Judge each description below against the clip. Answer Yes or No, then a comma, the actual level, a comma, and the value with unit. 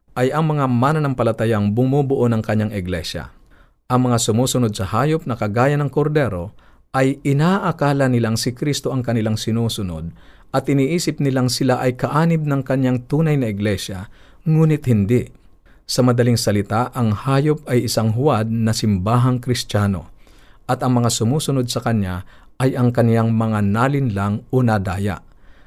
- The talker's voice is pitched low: Yes, low, 120 Hz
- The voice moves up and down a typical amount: Yes, average, 4.1 semitones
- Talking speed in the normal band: Yes, average, 145 wpm